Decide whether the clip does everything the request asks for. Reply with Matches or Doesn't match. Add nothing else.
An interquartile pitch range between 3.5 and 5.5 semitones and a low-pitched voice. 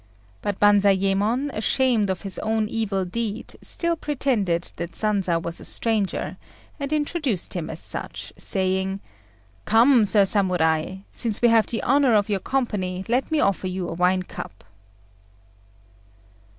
Doesn't match